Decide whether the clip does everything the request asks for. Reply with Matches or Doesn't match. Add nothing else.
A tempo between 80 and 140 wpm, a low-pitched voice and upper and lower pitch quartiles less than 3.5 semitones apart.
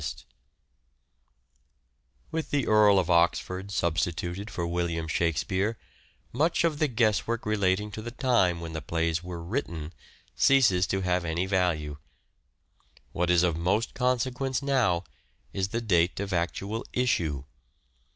Doesn't match